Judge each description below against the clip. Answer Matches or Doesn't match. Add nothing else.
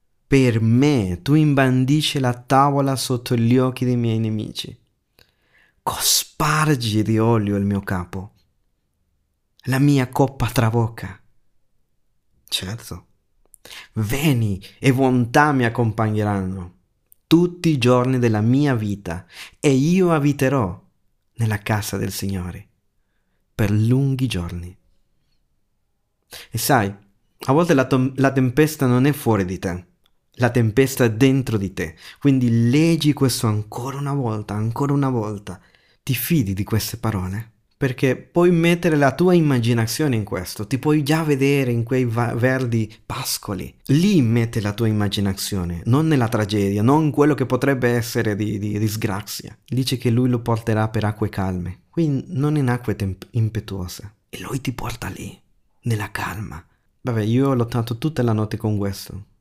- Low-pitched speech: Matches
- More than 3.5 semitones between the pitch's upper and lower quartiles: Matches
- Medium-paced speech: Matches